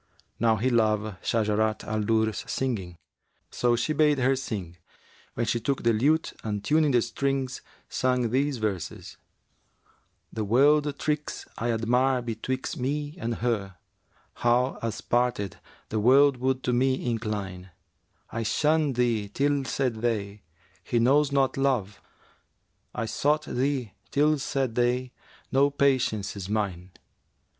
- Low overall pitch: Yes, low, 120 Hz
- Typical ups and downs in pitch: Yes, average, 3.9 semitones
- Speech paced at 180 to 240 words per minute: No, average, 140 wpm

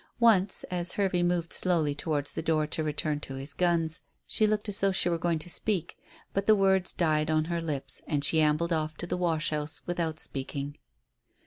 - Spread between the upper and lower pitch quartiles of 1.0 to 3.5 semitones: Yes, average, 2.8 semitones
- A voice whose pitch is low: No, medium, 165 Hz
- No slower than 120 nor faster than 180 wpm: No, fast, 205 wpm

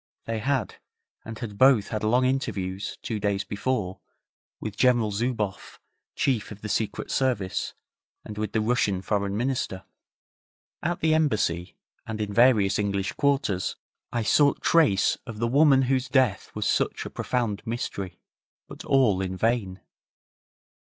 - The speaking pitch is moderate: No, low, 110 Hz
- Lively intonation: No, average, 4.3 semitones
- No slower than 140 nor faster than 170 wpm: Yes, average, 145 wpm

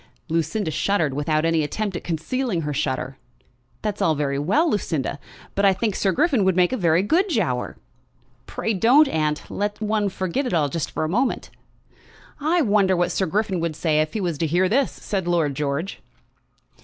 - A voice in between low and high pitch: Yes, medium, 180 Hz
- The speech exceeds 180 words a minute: Yes, average, 190 wpm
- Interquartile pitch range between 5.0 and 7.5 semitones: Yes, average, 5.3 semitones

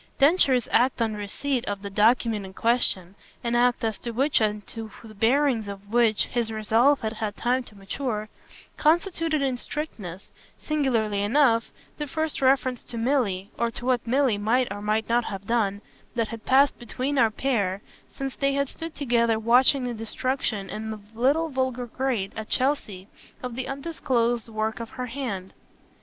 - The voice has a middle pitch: No, high, 235 Hz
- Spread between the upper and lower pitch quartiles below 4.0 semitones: Yes, average, 3.6 semitones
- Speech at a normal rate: Yes, average, 175 wpm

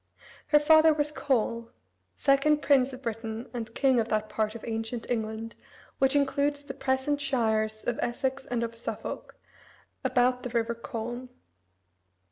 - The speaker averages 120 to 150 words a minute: Yes, average, 145 wpm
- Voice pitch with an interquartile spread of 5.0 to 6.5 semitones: No, average, 3.4 semitones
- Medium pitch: No, high, 245 Hz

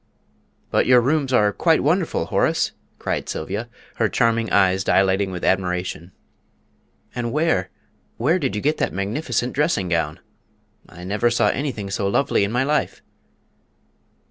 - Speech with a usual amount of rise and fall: No, wide, 6.0 semitones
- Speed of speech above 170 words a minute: No, average, 145 wpm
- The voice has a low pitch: Yes, low, 115 Hz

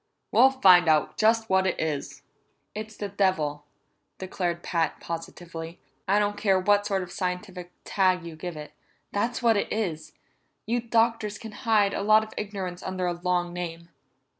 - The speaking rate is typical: Yes, average, 165 wpm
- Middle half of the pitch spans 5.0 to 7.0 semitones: No, average, 3.3 semitones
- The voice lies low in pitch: No, high, 190 Hz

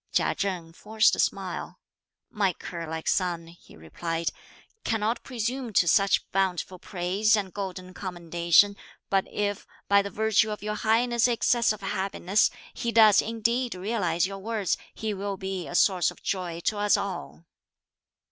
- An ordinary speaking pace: Yes, average, 155 wpm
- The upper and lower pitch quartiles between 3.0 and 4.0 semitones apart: Yes, average, 3.3 semitones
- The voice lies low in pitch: No, high, 195 Hz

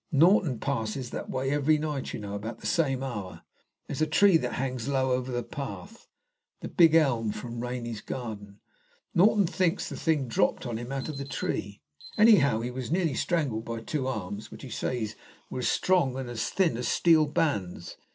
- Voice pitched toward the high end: No, low, 130 Hz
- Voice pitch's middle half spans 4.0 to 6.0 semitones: Yes, average, 5.1 semitones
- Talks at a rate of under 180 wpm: No, average, 190 wpm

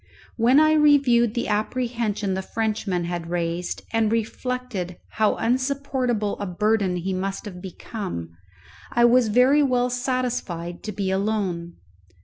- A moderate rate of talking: No, slow, 130 wpm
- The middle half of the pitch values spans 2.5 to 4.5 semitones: No, average, 5.0 semitones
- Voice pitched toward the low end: No, high, 215 Hz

